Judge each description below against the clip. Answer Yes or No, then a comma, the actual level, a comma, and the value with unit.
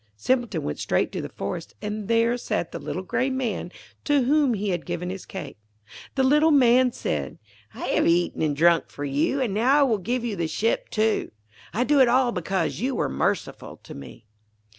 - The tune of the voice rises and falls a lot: Yes, wide, 6.6 semitones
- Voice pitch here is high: Yes, high, 220 Hz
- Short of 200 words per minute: No, fast, 205 wpm